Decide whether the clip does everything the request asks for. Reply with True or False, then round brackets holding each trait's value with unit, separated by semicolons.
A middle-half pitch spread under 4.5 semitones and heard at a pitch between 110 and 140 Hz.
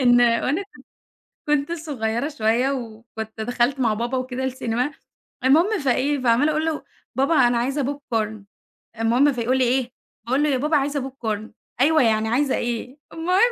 False (3.7 semitones; 255 Hz)